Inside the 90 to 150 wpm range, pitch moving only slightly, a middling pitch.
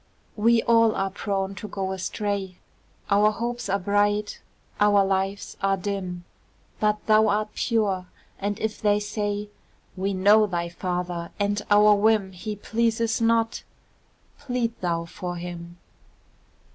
No: slow, 135 wpm; narrow, 2.1 semitones; high, 205 Hz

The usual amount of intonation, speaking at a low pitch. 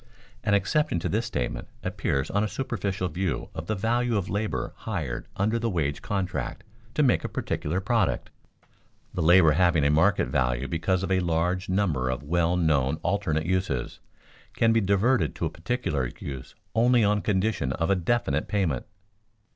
Yes: average, 4.7 semitones; very low, 90 Hz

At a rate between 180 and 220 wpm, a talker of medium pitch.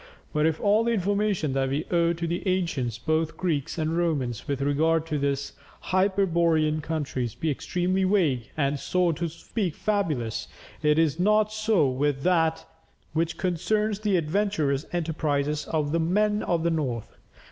No: average, 160 wpm; medium, 165 Hz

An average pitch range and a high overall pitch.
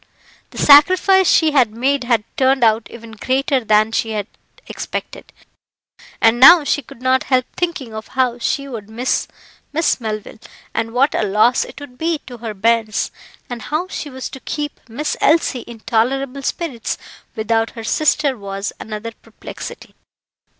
Yes: average, 3.9 semitones; high, 245 Hz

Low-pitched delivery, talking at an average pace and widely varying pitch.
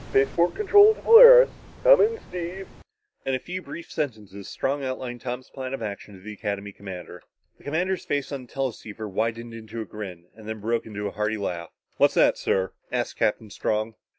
Yes: low, 115 Hz; average, 190 wpm; wide, 6.3 semitones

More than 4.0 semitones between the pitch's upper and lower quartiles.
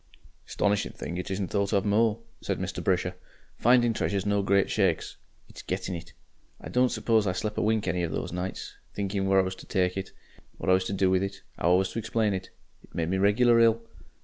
No: narrow, 2.4 semitones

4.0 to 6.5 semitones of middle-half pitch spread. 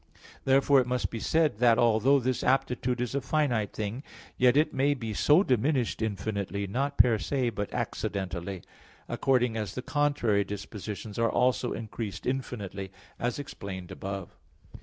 Yes: average, 4.5 semitones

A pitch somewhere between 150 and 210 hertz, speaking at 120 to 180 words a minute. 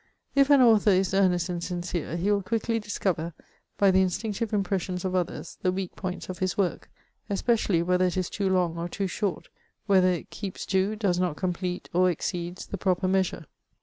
No: medium, 185 Hz; average, 190 wpm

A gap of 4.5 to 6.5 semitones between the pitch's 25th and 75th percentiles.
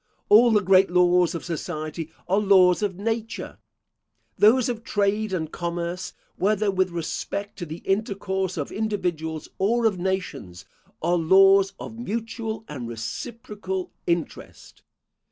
No: average, 3.5 semitones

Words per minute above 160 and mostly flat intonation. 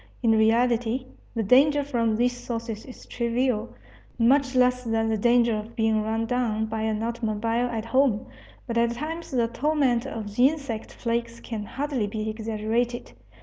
No: average, 155 wpm; narrow, 2.1 semitones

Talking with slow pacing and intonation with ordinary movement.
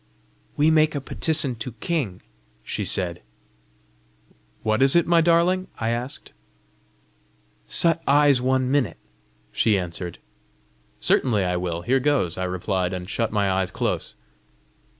No: slow, 130 wpm; wide, 7.9 semitones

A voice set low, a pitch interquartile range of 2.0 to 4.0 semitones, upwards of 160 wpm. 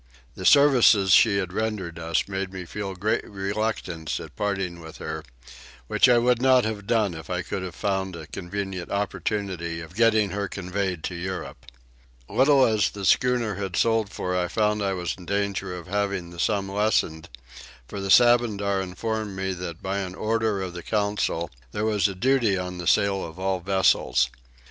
Yes: very low, 95 Hz; average, 2.8 semitones; average, 180 wpm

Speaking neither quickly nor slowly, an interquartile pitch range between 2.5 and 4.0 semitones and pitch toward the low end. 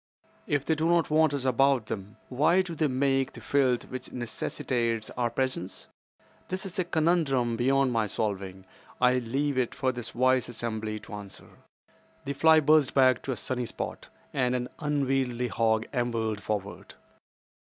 Yes: average, 165 wpm; average, 3.5 semitones; low, 130 Hz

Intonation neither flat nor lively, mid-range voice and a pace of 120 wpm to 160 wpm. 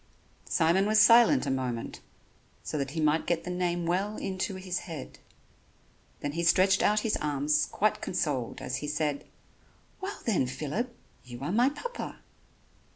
No: wide, 6.0 semitones; medium, 175 Hz; average, 155 wpm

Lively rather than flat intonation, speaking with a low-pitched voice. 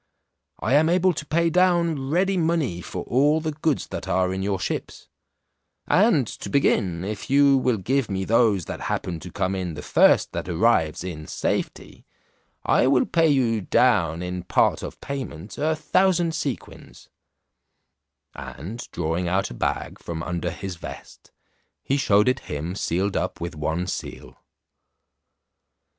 Yes: wide, 8.7 semitones; low, 115 Hz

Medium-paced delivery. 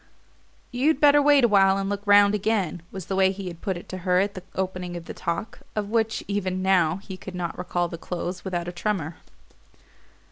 No: fast, 210 wpm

